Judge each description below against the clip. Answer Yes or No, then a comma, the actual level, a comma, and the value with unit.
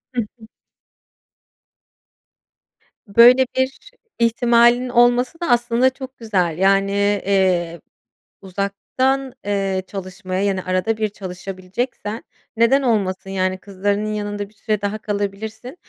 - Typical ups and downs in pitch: Yes, average, 3.7 semitones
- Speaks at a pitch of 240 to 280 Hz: No, high, 205 Hz